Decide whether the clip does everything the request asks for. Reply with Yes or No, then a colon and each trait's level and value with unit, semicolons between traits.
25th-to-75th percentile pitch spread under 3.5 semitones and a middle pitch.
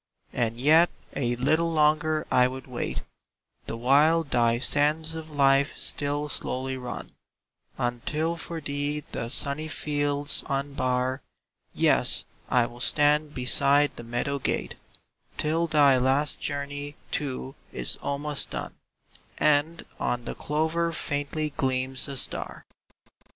Yes: average, 2.7 semitones; medium, 145 Hz